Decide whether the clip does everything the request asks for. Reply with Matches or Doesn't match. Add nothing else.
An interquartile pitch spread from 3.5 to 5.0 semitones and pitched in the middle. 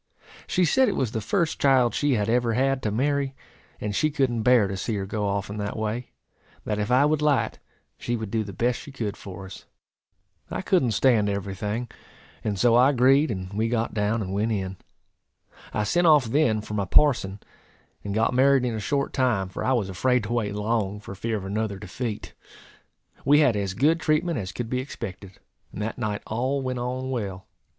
Doesn't match